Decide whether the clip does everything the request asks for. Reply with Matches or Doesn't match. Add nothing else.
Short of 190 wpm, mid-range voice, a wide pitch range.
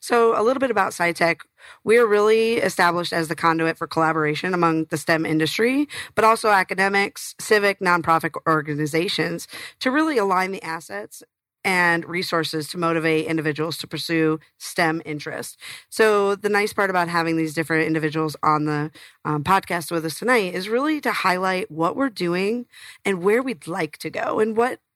Doesn't match